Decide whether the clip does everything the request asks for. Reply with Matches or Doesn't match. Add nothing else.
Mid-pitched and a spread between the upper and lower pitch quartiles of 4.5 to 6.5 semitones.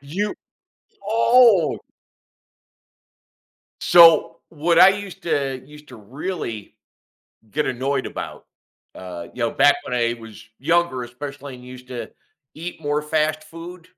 Matches